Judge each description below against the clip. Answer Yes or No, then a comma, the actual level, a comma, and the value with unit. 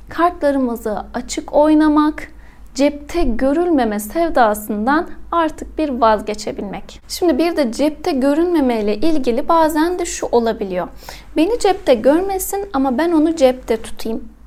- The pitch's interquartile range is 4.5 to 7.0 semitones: Yes, average, 5.2 semitones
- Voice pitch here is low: No, very high, 290 Hz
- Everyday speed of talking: Yes, average, 115 wpm